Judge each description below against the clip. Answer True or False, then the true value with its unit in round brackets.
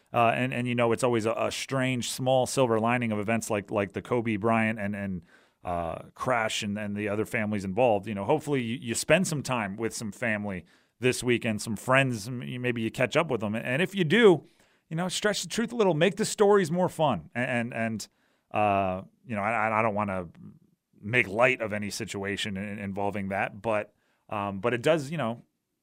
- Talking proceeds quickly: True (210 wpm)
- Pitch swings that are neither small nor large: True (3.8 semitones)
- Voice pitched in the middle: False (115 Hz)